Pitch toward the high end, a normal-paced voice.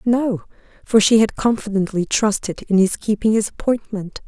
Yes: high, 210 Hz; average, 155 wpm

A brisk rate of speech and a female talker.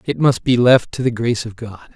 No: fast, 275 wpm; male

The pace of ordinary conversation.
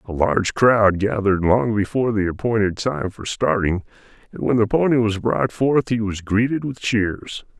Yes: average, 180 wpm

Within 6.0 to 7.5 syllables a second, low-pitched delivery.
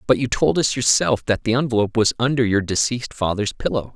Yes: 6.1 syllables/s; low, 115 Hz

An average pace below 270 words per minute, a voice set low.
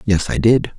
Yes: fast, 230 wpm; low, 105 Hz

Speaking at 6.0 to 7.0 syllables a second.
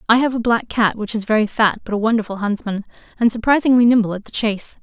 Yes: 6.5 syllables/s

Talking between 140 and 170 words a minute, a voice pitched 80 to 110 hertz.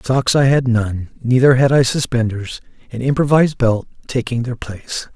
No: average, 165 wpm; low, 125 Hz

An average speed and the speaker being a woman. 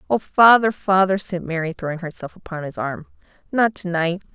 Yes: average, 165 wpm; female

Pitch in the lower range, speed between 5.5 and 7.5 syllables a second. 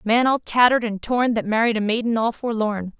No: high, 225 Hz; 5.6 syllables/s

